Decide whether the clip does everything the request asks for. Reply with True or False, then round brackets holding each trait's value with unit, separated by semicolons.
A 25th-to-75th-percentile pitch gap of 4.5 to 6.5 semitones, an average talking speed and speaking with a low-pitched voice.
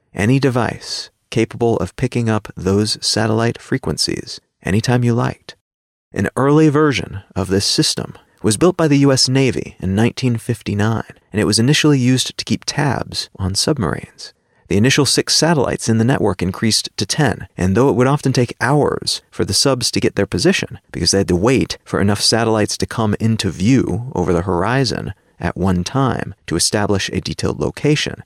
True (4.9 semitones; 175 wpm; 115 Hz)